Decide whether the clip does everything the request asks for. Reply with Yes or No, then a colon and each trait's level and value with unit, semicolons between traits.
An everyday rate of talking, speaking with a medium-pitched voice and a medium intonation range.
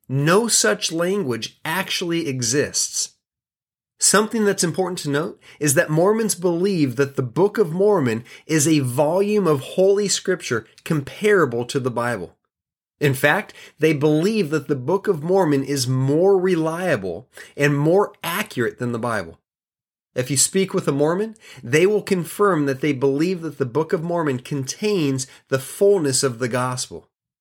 No: average, 155 wpm; medium, 155 Hz; wide, 5.7 semitones